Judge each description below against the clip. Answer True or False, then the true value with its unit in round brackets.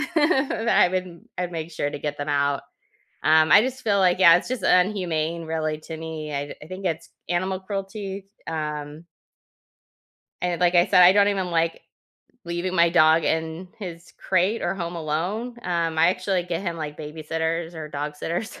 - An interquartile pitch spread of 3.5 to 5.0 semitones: False (2.9 semitones)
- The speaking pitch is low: False (170 Hz)